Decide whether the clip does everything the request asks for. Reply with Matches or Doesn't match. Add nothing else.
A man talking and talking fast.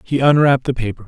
Matches